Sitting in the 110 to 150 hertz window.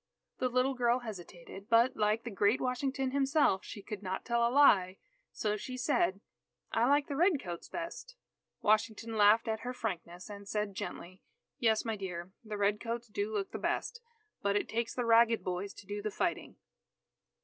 No: high, 220 Hz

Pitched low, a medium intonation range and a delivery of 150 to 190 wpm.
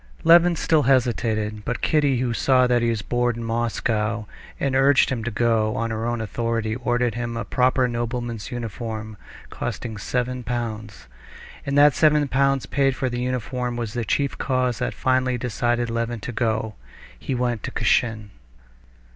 No: low, 120 Hz; narrow, 2.0 semitones; average, 165 wpm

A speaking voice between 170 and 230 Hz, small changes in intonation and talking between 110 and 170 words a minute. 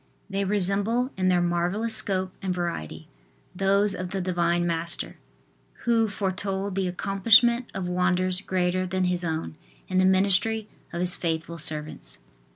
Yes: medium, 185 Hz; narrow, 2.2 semitones; average, 145 wpm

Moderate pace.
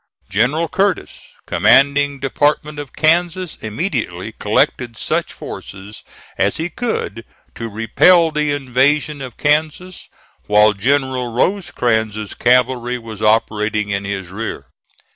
No: slow, 110 wpm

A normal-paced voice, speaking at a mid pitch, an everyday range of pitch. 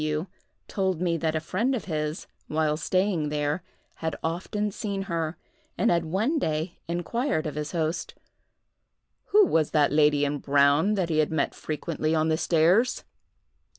Yes: average, 160 wpm; medium, 160 Hz; average, 3.5 semitones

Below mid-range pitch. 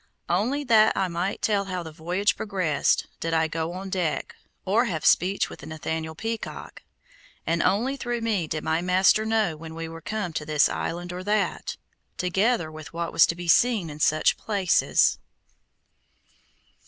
No: medium, 180 Hz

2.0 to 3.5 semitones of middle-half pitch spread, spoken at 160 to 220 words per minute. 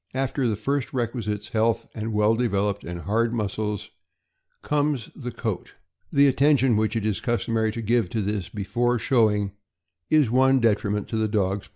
Yes: average, 2.9 semitones; average, 170 wpm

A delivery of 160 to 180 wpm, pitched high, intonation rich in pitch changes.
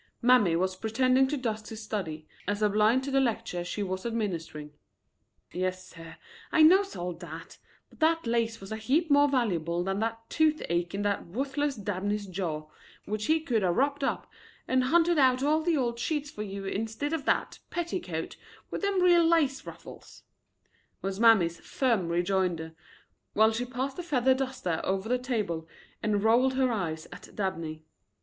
Yes: average, 170 wpm; high, 220 Hz; wide, 6.4 semitones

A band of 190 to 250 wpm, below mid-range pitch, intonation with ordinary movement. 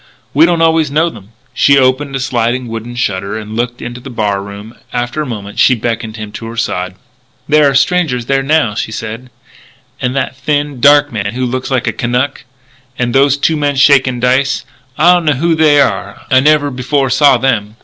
Yes: average, 200 wpm; low, 130 Hz; average, 3.7 semitones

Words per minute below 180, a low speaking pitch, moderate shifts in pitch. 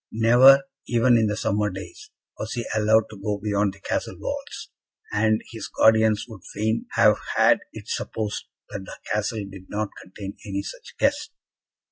No: average, 165 wpm; low, 105 Hz; narrow, 1.8 semitones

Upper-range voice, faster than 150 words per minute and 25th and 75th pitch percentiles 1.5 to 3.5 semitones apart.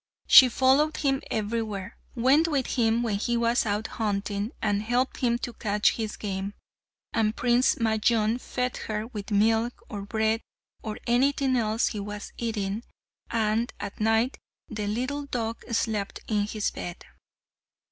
No: high, 225 Hz; average, 145 wpm; narrow, 2.4 semitones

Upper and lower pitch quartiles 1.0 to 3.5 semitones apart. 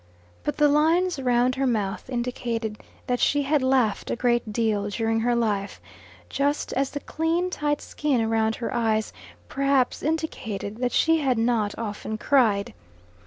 No: average, 4.3 semitones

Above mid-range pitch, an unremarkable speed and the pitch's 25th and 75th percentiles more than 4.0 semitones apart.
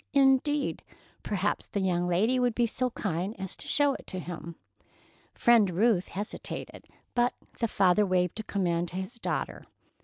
Yes: high, 205 Hz; average, 160 wpm; average, 5.0 semitones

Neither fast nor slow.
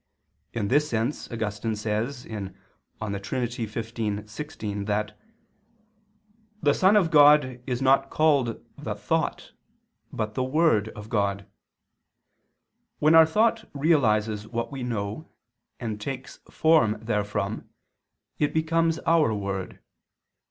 No: slow, 115 wpm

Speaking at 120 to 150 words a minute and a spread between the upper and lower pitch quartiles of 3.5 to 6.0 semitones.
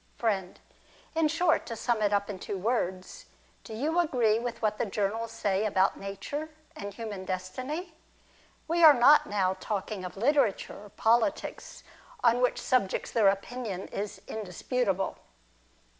Yes: average, 145 wpm; average, 4.3 semitones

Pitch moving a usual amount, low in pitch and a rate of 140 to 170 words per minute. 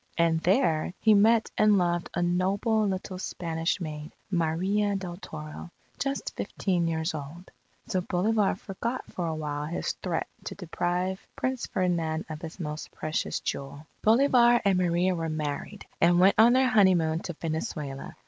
No: average, 3.8 semitones; medium, 175 Hz; average, 155 wpm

